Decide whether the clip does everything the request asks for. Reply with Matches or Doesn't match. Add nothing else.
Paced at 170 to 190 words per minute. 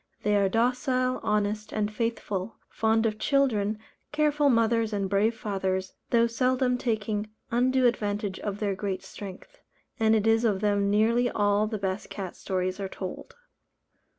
Doesn't match